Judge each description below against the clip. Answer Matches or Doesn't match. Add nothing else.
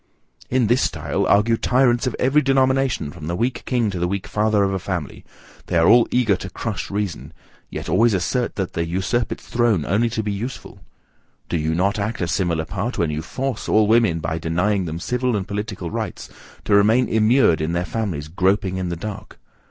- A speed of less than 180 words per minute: Doesn't match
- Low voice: Matches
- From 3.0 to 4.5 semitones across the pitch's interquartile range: Doesn't match